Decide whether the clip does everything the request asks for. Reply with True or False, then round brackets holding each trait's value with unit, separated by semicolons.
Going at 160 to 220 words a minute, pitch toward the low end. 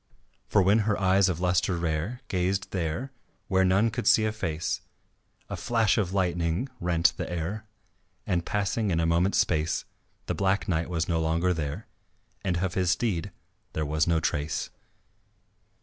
True (165 wpm; 90 Hz)